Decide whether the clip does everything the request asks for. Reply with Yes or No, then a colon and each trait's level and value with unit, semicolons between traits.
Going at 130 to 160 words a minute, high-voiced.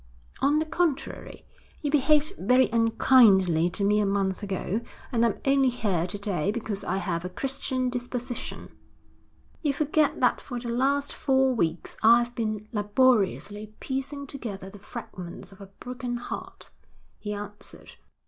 Yes: average, 150 wpm; high, 230 Hz